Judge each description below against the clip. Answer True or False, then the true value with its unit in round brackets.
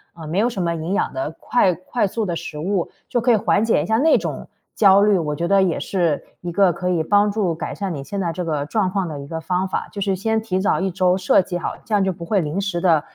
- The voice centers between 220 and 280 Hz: False (185 Hz)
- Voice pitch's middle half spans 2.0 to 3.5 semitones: True (3.2 semitones)